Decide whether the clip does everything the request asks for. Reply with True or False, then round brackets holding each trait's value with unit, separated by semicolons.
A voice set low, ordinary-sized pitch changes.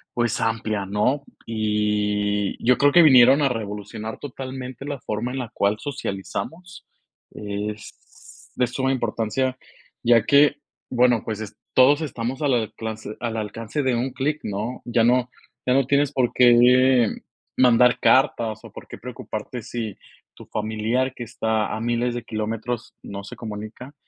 True (120 Hz; 3.2 semitones)